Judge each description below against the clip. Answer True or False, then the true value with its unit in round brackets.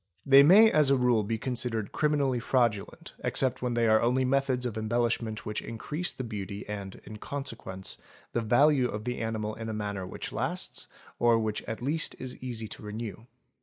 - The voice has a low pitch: True (115 Hz)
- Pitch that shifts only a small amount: False (3.2 semitones)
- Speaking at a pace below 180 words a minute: False (185 wpm)